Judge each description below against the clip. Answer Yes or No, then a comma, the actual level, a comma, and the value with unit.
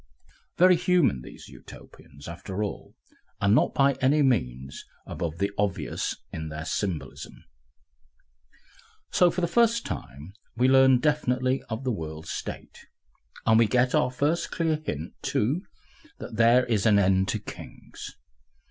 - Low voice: Yes, low, 115 Hz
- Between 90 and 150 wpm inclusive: Yes, average, 140 wpm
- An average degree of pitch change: No, wide, 8.3 semitones